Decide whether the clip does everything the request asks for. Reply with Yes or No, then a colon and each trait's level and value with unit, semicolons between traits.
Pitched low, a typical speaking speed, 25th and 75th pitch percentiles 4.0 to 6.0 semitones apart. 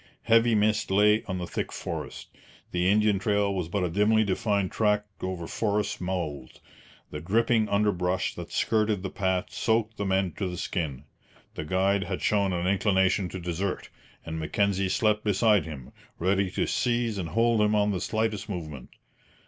No: low, 100 Hz; average, 170 wpm; average, 2.7 semitones